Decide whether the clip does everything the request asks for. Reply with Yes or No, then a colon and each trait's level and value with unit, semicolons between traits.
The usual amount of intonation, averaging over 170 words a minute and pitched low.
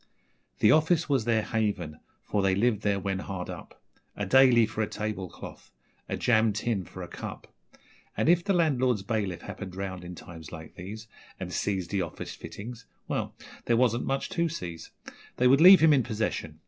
Yes: average, 4.9 semitones; average, 185 wpm; low, 110 Hz